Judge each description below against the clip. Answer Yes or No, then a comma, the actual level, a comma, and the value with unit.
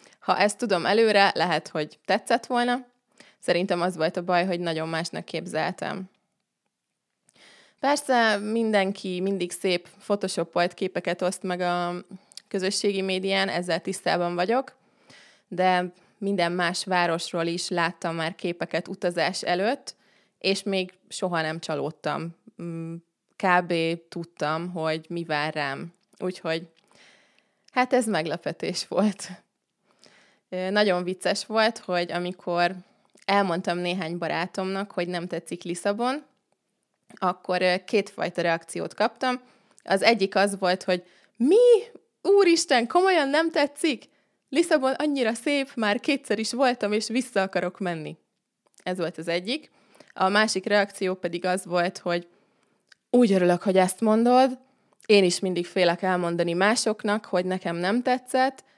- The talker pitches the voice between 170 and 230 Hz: Yes, high, 190 Hz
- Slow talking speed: No, average, 120 wpm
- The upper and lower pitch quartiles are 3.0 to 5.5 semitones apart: Yes, average, 3.8 semitones